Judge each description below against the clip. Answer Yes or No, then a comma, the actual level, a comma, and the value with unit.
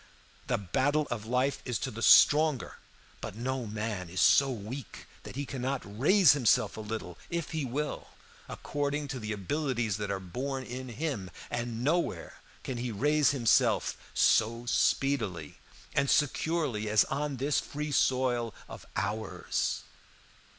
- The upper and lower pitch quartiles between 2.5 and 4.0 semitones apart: No, average, 4.5 semitones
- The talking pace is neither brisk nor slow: Yes, average, 145 wpm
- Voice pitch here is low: Yes, low, 125 Hz